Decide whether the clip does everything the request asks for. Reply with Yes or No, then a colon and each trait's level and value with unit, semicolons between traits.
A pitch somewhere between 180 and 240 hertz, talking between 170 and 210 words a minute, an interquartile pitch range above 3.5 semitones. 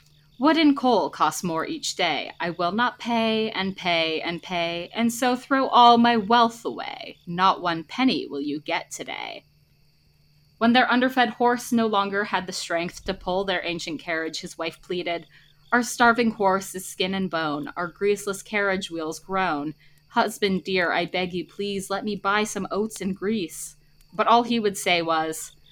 Yes: high, 190 Hz; average, 180 wpm; wide, 5.5 semitones